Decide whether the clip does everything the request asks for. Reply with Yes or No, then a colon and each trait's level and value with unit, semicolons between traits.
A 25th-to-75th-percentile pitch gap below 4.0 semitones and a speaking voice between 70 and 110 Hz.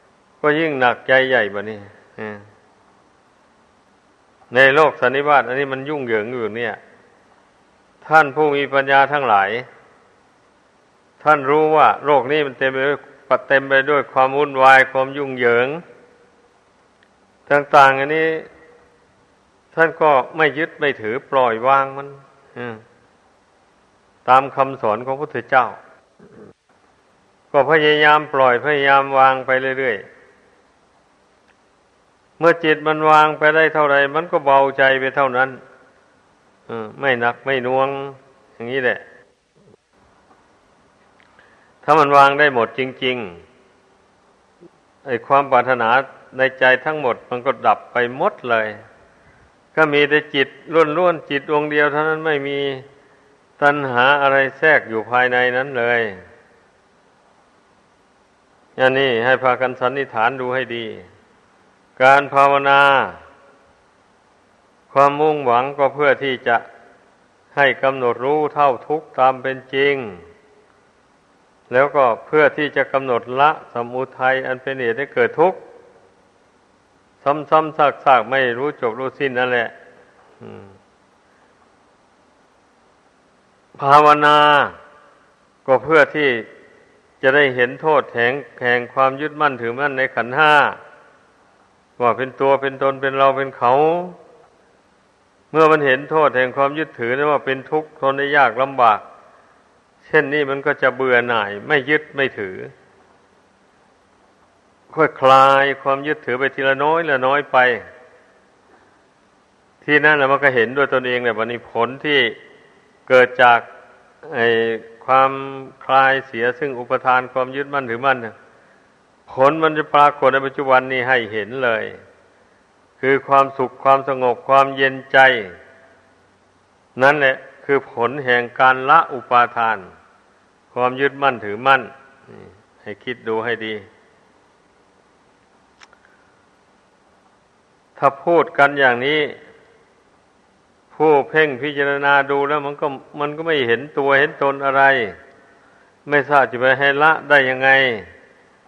No: narrow, 2.5 semitones; low, 135 Hz